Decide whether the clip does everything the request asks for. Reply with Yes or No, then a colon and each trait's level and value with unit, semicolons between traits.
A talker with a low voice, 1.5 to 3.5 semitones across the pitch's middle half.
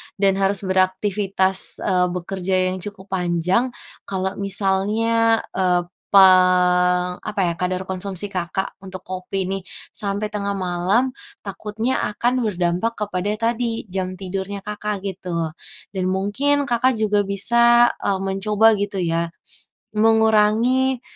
No: high, 195 Hz; narrow, 2.5 semitones